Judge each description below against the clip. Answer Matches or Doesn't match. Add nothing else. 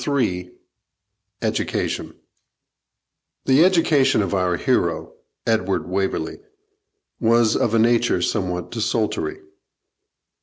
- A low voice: Matches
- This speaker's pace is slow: Matches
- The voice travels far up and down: Matches